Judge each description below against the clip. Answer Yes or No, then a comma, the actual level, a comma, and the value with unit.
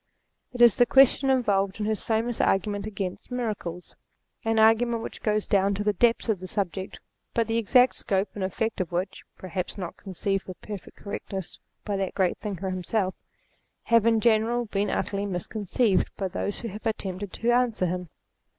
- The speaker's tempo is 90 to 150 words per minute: No, average, 180 wpm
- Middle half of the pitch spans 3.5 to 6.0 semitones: No, average, 3.0 semitones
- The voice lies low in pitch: No, high, 205 Hz